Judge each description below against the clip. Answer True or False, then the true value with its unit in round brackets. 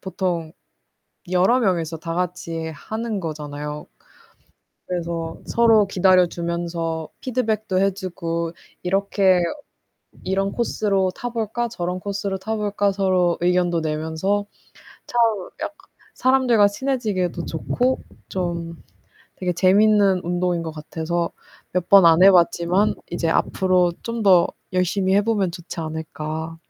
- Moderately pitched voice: True (180 Hz)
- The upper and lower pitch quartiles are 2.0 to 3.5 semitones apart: True (3.2 semitones)